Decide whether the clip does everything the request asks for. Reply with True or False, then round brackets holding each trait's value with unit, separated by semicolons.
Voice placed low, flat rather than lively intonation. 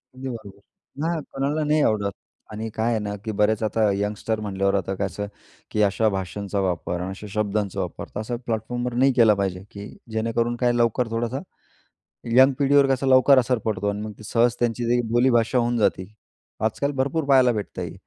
False (110 Hz; 3.3 semitones)